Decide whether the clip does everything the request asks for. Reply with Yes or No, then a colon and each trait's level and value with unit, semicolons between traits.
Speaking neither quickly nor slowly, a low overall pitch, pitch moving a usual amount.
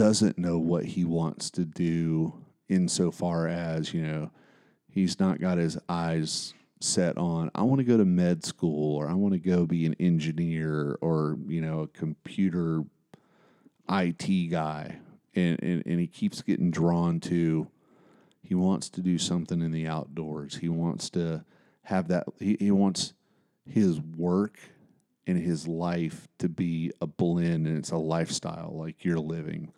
No: average, 160 wpm; very low, 85 Hz; narrow, 1.9 semitones